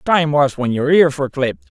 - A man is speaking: Yes, male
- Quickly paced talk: Yes, fast, 235 wpm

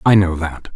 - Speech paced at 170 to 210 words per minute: No, fast, 240 wpm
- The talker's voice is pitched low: Yes, very low, 90 Hz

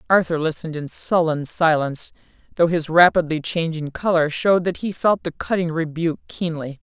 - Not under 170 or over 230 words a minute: No, average, 155 wpm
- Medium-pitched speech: Yes, medium, 165 Hz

